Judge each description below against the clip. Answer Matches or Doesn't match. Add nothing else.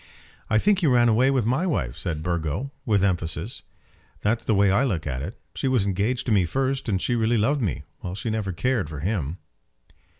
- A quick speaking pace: Matches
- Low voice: Matches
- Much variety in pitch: Matches